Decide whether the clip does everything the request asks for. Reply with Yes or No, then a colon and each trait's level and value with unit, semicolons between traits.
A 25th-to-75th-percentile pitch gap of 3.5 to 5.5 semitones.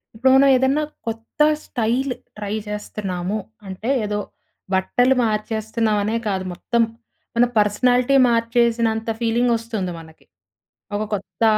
No: narrow, 2.6 semitones